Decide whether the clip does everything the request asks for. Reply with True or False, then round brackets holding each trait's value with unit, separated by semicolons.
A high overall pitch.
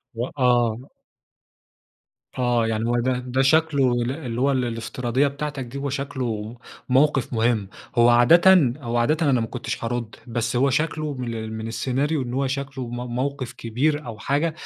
False (125 Hz)